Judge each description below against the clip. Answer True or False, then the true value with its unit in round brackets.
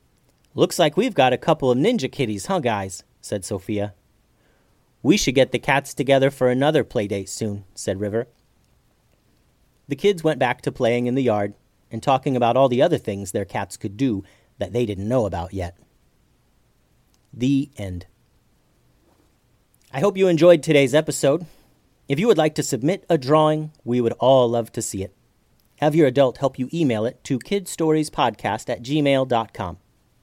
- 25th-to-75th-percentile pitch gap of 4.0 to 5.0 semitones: False (5.5 semitones)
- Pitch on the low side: True (125 Hz)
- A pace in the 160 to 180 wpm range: True (170 wpm)